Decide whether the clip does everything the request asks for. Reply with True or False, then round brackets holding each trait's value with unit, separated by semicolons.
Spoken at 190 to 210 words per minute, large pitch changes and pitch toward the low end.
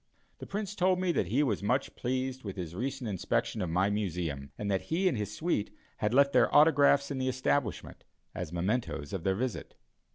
True (200 wpm; 6.5 semitones; 120 Hz)